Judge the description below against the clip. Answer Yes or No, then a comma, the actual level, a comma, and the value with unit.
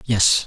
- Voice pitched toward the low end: Yes, low, 105 Hz